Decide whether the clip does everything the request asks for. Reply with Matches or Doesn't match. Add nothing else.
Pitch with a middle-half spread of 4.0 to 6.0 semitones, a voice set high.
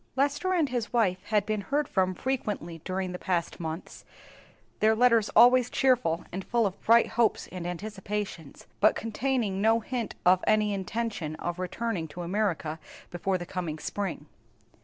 Matches